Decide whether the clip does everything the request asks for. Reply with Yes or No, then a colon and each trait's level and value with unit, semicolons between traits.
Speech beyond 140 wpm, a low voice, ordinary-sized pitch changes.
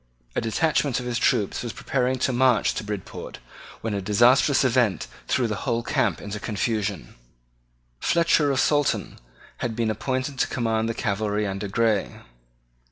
Yes: average, 155 wpm; low, 115 Hz; average, 3.7 semitones